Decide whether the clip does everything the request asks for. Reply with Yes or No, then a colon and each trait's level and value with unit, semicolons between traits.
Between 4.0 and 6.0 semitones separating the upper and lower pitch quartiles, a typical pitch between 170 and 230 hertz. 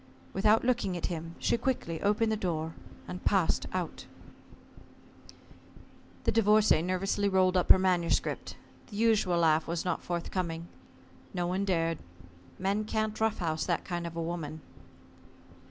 No: average, 3.5 semitones; medium, 185 Hz